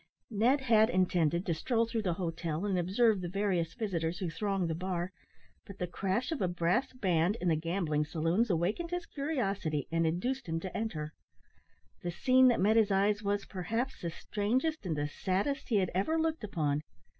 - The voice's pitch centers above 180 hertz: Yes, high, 190 Hz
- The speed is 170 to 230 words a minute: Yes, average, 190 wpm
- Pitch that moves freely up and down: No, average, 4.9 semitones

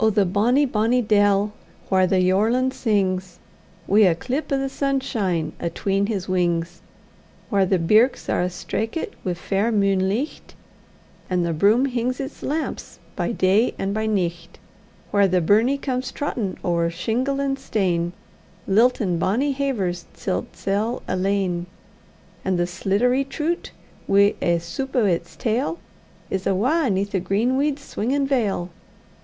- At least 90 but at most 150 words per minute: Yes, average, 145 wpm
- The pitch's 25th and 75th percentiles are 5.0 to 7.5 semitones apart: Yes, wide, 5.4 semitones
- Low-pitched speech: No, high, 205 Hz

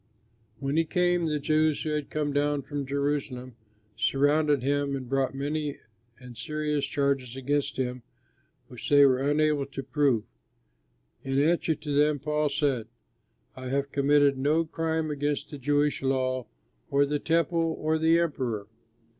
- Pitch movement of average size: No, narrow, 2.0 semitones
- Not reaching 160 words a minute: Yes, average, 150 wpm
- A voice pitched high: No, medium, 145 Hz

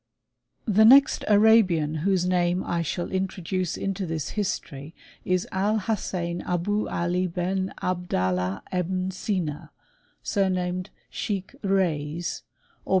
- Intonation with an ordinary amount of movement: No, narrow, 2.2 semitones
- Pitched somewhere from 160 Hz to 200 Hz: Yes, medium, 185 Hz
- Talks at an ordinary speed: No, slow, 120 wpm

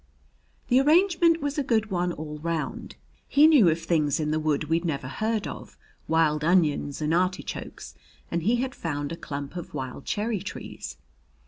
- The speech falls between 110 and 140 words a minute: No, average, 175 wpm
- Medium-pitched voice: Yes, medium, 170 Hz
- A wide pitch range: Yes, wide, 6.9 semitones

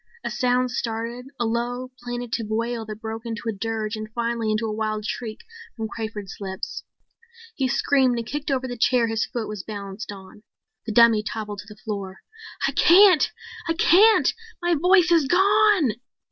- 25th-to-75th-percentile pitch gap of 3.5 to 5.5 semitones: No, average, 3.1 semitones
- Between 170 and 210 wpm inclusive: Yes, average, 175 wpm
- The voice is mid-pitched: No, high, 230 Hz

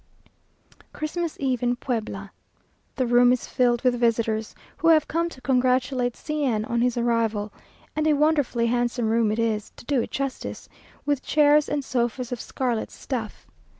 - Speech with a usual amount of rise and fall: Yes, average, 3.3 semitones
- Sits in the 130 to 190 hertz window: No, high, 245 Hz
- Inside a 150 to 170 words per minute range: Yes, average, 165 wpm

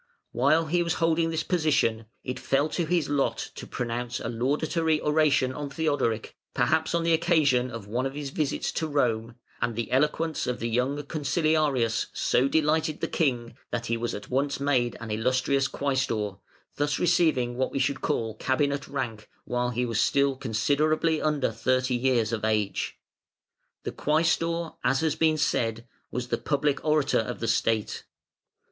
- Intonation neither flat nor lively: Yes, average, 4.4 semitones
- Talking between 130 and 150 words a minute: No, average, 165 wpm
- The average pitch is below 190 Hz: Yes, low, 135 Hz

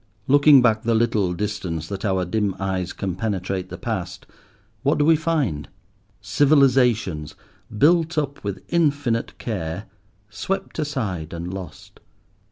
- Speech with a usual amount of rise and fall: No, wide, 7.3 semitones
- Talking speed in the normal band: No, slow, 130 wpm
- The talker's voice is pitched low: Yes, low, 110 Hz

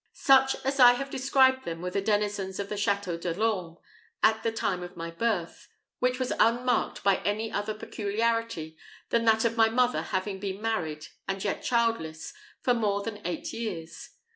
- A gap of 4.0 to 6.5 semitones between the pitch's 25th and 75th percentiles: No, average, 3.6 semitones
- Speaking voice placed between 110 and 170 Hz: No, high, 210 Hz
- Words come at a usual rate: Yes, average, 180 wpm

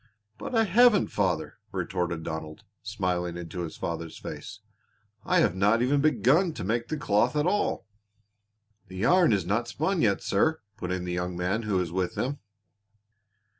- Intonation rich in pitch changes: Yes, wide, 8.4 semitones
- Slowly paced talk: No, average, 170 wpm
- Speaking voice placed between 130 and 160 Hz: No, low, 100 Hz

